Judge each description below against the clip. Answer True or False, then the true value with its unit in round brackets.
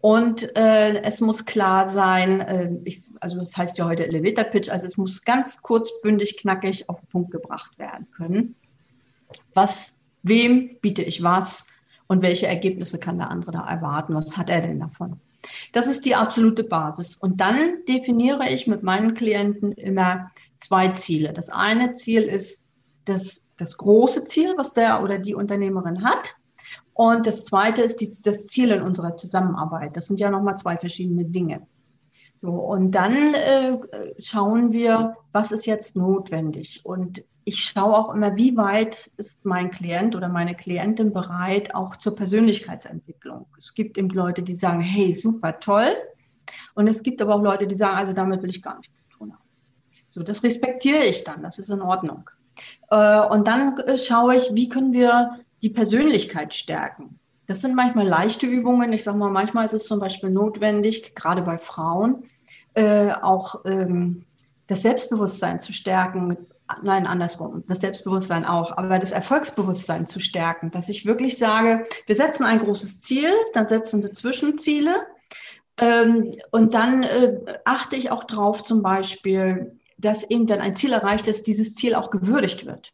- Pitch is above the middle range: True (200 Hz)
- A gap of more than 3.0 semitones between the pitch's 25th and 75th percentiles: True (3.8 semitones)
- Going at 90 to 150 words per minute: False (170 wpm)